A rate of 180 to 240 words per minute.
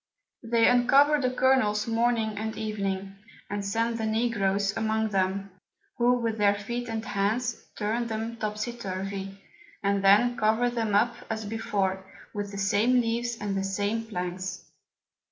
No: average, 150 wpm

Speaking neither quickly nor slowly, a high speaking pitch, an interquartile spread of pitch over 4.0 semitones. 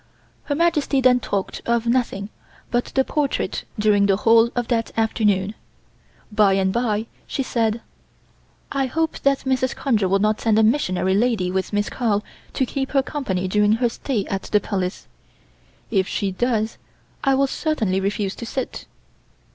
Yes: average, 165 wpm; high, 225 Hz; average, 4.4 semitones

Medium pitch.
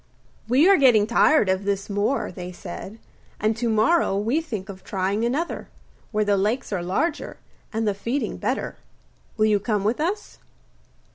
No: high, 215 Hz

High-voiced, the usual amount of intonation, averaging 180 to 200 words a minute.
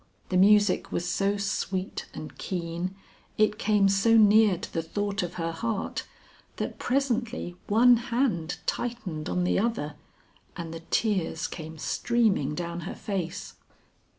No: high, 195 Hz; average, 4.3 semitones; average, 140 wpm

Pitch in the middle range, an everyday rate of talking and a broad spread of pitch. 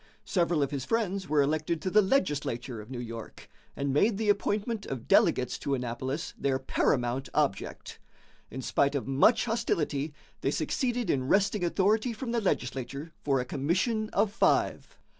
Yes: medium, 150 Hz; average, 160 wpm; wide, 7.6 semitones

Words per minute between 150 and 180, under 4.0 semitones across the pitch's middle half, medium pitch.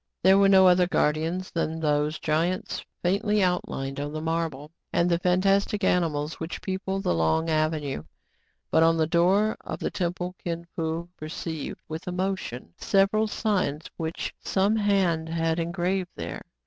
Yes: average, 155 wpm; average, 3.1 semitones; medium, 170 Hz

